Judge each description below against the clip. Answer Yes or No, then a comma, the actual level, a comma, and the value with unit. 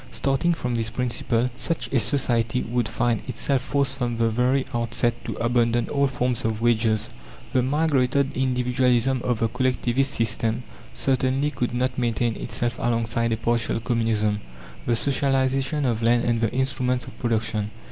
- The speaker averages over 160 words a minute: No, average, 155 wpm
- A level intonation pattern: Yes, narrow, 2.3 semitones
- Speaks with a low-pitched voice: Yes, low, 120 Hz